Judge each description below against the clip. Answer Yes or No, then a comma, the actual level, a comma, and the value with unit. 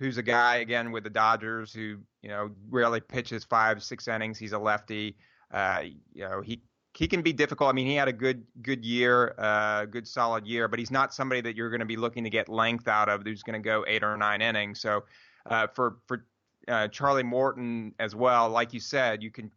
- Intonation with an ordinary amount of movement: No, narrow, 2.2 semitones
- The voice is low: Yes, low, 115 Hz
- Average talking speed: No, fast, 230 wpm